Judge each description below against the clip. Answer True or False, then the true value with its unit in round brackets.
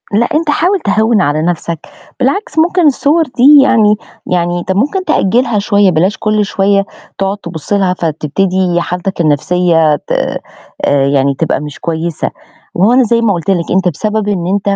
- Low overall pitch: False (195 Hz)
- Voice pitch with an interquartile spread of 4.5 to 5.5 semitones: True (4.8 semitones)